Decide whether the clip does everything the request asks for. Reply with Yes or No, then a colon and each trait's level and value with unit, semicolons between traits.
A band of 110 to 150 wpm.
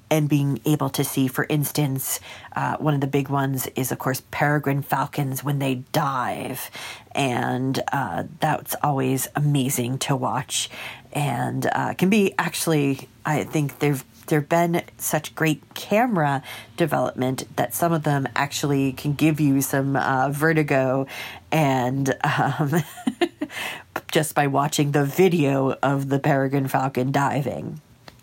Yes: average, 140 wpm